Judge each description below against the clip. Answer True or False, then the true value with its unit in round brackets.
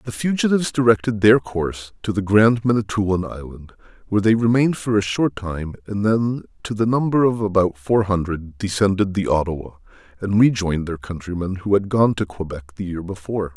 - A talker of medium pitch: False (100 Hz)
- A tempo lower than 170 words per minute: False (180 wpm)